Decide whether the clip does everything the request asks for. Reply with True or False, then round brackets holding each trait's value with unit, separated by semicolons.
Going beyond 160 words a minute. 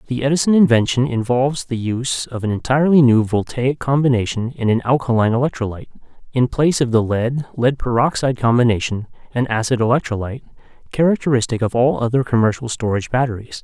False (150 wpm)